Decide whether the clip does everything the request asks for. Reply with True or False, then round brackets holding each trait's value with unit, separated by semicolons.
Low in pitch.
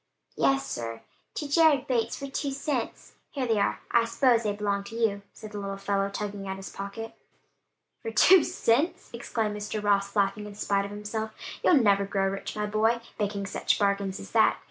False (210 Hz)